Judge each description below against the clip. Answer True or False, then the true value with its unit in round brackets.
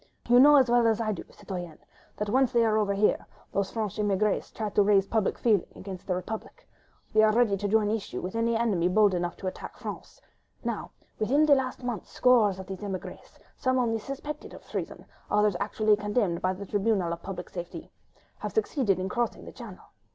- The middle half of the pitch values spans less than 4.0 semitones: True (3.3 semitones)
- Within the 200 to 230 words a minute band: True (205 wpm)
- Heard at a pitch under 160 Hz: False (210 Hz)